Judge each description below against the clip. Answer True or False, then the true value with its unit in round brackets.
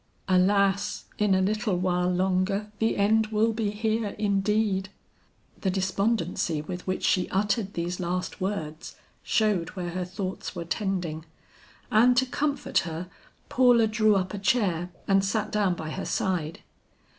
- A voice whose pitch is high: True (195 Hz)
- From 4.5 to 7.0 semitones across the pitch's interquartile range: False (2.9 semitones)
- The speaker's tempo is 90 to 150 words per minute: True (145 wpm)